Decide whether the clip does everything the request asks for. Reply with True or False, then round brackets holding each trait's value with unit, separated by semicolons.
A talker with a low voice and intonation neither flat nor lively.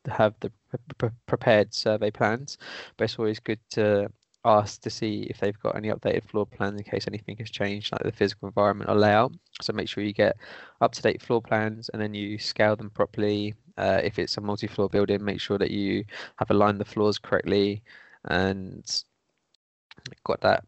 False (105 Hz; 1.6 semitones)